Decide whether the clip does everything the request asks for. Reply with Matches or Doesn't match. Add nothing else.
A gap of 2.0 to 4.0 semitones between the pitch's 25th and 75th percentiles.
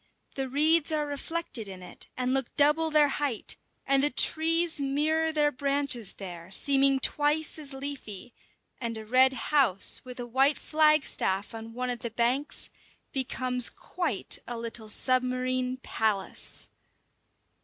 Matches